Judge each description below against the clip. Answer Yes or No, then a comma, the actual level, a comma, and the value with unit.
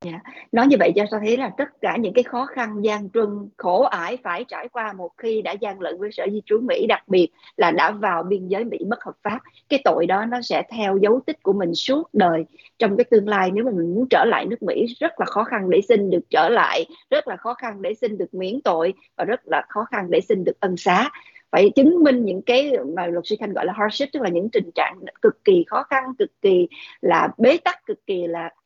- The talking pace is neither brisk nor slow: No, fast, 260 wpm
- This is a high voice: Yes, high, 230 Hz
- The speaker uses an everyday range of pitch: No, wide, 6.0 semitones